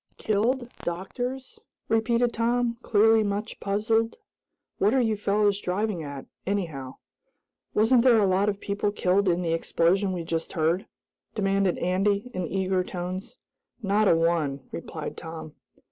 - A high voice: Yes, high, 200 Hz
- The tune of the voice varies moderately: Yes, average, 3.7 semitones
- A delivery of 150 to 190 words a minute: No, slow, 135 wpm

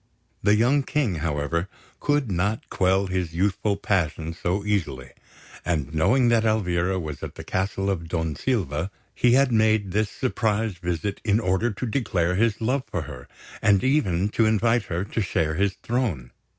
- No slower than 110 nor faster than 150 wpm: No, average, 165 wpm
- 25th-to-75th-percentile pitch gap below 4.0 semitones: No, average, 4.7 semitones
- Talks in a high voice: No, low, 100 Hz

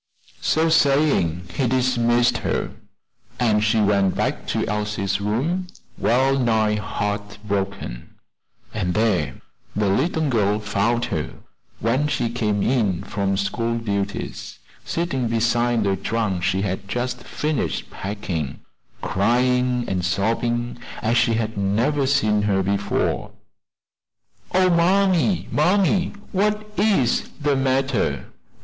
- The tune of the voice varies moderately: Yes, average, 4.8 semitones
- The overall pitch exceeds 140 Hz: No, low, 115 Hz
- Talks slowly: Yes, slow, 115 wpm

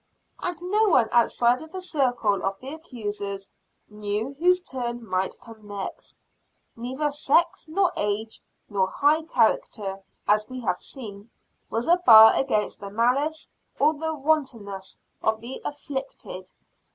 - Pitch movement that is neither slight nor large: No, wide, 6.4 semitones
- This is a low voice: No, high, 240 Hz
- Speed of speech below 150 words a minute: Yes, average, 140 wpm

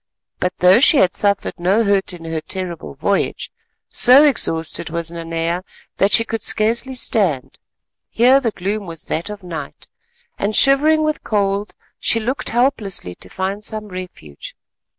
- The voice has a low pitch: No, high, 200 Hz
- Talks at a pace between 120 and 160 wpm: Yes, average, 150 wpm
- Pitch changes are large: No, average, 4.9 semitones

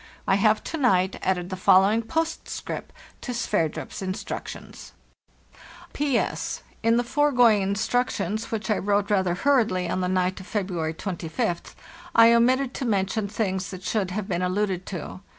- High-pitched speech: Yes, high, 200 Hz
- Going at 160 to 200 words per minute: No, average, 145 wpm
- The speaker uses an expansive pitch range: No, average, 3.6 semitones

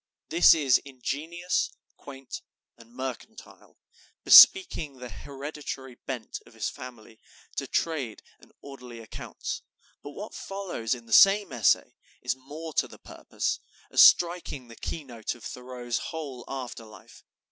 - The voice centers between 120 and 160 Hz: Yes, low, 135 Hz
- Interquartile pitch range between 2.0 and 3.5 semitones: No, average, 4.7 semitones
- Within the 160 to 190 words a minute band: No, slow, 135 wpm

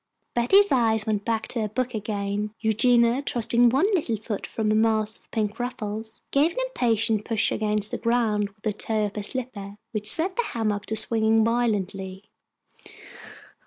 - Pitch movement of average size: No, narrow, 2.3 semitones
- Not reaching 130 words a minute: No, average, 170 wpm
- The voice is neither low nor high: No, high, 220 Hz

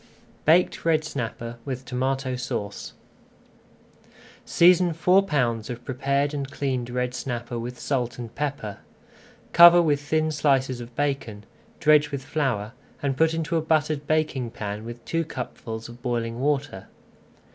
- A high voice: No, low, 135 Hz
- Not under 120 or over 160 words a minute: Yes, average, 140 wpm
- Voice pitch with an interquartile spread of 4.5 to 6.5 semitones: No, average, 4.0 semitones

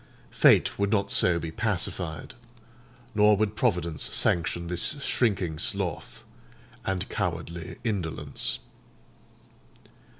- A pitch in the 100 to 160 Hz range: No, very low, 90 Hz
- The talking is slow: Yes, slow, 95 wpm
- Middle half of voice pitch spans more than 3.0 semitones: Yes, average, 3.7 semitones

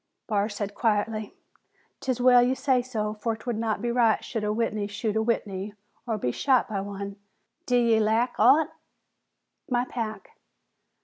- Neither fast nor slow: Yes, average, 160 wpm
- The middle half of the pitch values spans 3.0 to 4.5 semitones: No, narrow, 2.5 semitones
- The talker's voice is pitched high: Yes, high, 220 Hz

